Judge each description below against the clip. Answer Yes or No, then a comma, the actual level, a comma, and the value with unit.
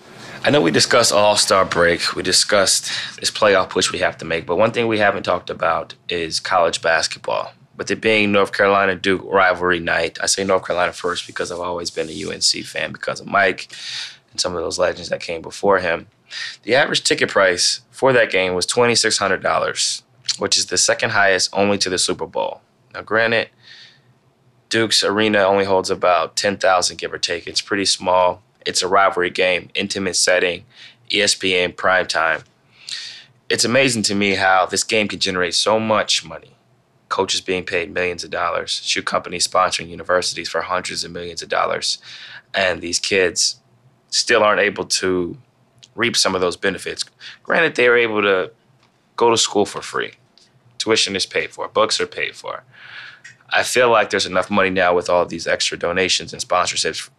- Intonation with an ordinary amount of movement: Yes, average, 3.4 semitones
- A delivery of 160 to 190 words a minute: Yes, average, 180 wpm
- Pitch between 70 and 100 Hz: Yes, very low, 95 Hz